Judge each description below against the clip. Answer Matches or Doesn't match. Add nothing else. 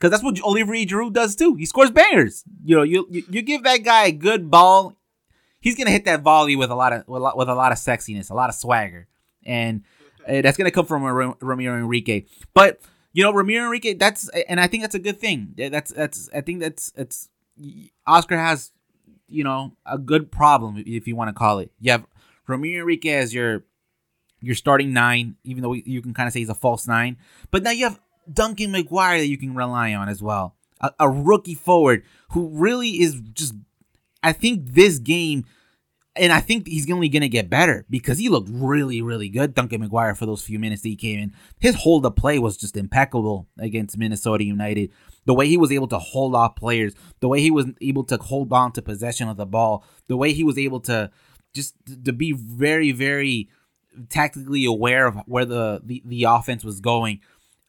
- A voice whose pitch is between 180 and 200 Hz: Doesn't match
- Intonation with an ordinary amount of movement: Doesn't match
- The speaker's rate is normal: Doesn't match